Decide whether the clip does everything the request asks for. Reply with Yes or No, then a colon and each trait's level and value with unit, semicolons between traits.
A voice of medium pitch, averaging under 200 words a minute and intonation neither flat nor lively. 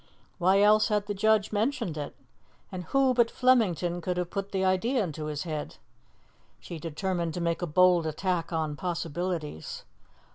Yes: medium, 180 Hz; average, 160 wpm; average, 3.8 semitones